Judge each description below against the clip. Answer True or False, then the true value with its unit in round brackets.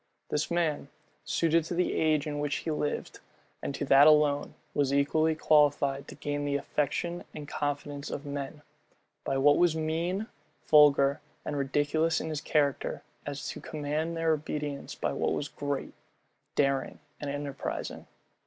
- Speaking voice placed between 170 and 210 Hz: False (145 Hz)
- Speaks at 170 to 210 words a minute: False (155 wpm)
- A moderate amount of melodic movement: False (1.7 semitones)